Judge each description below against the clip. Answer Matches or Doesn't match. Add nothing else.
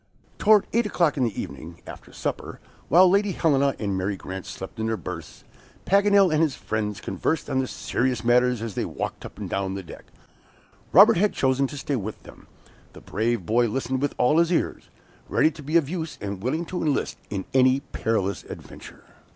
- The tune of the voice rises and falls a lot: Matches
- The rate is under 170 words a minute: Doesn't match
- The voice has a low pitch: Matches